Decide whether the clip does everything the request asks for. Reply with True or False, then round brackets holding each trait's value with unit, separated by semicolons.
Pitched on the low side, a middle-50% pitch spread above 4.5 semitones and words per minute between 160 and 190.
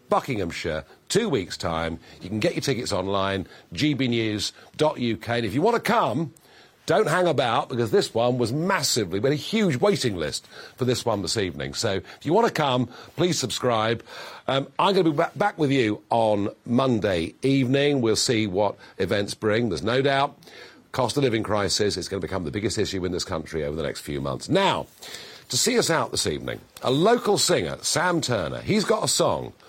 False (125 Hz; 5.3 semitones; 200 wpm)